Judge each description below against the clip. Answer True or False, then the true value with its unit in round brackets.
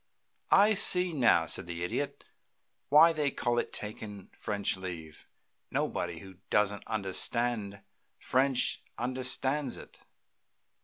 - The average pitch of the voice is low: True (110 Hz)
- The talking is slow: True (110 wpm)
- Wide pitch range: True (5.8 semitones)